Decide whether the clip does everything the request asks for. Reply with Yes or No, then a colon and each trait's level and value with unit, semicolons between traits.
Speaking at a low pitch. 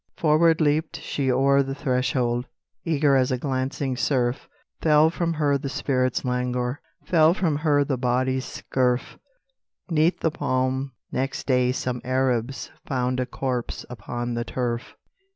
Yes: low, 130 Hz